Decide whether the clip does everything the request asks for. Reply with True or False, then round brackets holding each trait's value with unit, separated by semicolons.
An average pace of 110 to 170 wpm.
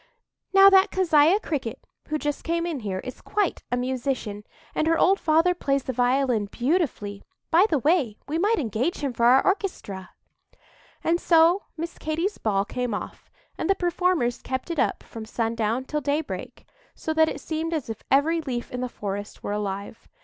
False (180 wpm)